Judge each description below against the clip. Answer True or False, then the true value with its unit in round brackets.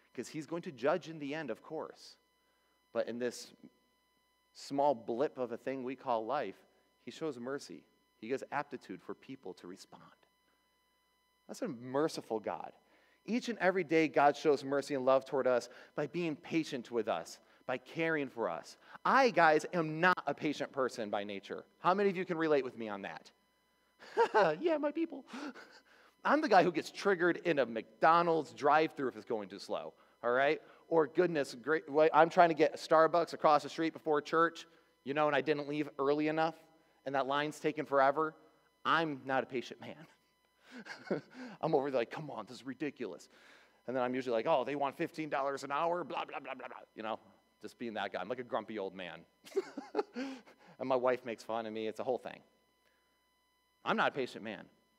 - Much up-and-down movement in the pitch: False (3.8 semitones)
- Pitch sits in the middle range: True (150 Hz)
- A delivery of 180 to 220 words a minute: True (195 wpm)